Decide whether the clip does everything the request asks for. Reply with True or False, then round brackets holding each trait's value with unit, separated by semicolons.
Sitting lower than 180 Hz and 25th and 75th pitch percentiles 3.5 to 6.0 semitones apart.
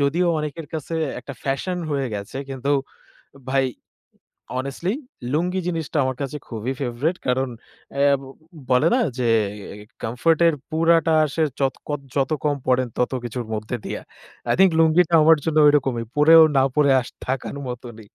True (140 Hz; 4.1 semitones)